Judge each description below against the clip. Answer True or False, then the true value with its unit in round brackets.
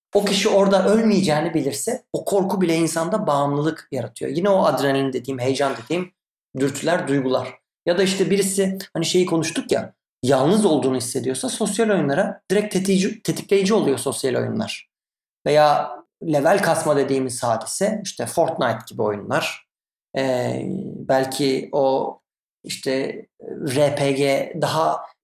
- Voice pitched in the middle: True (160 Hz)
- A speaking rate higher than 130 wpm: False (125 wpm)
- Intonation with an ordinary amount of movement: False (6.2 semitones)